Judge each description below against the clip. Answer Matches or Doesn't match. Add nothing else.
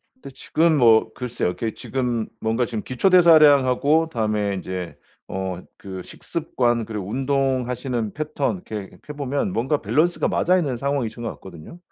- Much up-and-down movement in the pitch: Doesn't match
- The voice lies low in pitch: Matches